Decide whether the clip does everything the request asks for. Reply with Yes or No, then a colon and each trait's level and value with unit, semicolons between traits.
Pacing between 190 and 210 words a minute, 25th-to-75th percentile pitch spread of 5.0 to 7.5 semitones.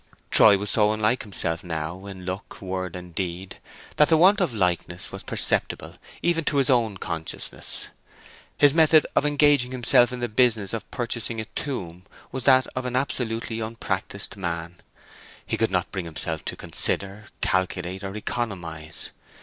No: average, 160 wpm; wide, 5.5 semitones